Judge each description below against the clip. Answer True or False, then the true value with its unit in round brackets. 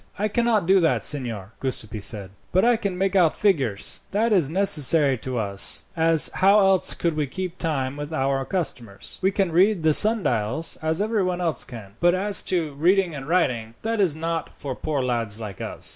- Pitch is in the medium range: True (160 Hz)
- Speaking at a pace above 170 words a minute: True (190 wpm)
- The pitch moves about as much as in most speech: False (6.5 semitones)